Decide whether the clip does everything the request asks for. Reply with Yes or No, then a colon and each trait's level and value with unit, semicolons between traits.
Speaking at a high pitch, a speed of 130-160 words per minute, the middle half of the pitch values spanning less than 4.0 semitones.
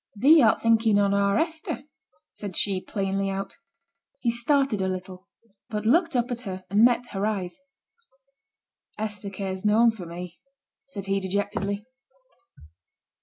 Yes: high, 205 Hz; average, 140 wpm; average, 3.1 semitones